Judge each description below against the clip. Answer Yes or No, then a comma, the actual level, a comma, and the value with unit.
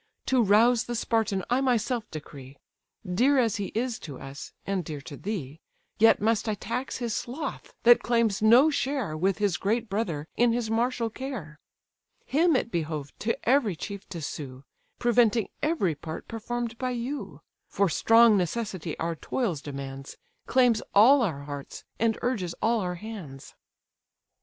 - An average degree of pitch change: No, wide, 6.3 semitones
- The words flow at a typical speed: Yes, average, 155 wpm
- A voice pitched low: No, high, 220 Hz